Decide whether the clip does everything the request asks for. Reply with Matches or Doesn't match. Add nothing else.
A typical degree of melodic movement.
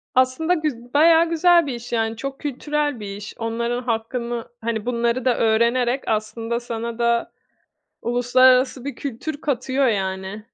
Matches